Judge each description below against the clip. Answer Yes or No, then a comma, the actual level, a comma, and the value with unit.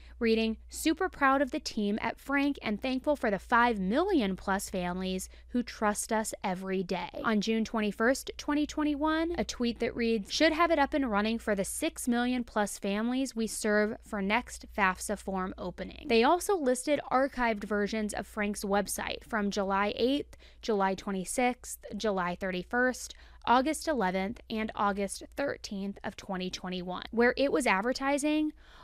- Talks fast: No, average, 155 wpm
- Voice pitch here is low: No, high, 225 Hz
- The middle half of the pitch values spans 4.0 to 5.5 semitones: Yes, average, 5.0 semitones